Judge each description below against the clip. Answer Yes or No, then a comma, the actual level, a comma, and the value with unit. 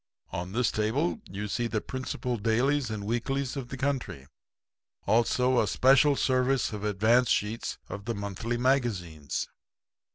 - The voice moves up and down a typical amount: Yes, average, 3.8 semitones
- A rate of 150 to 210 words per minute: No, average, 140 wpm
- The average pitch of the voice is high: No, low, 120 Hz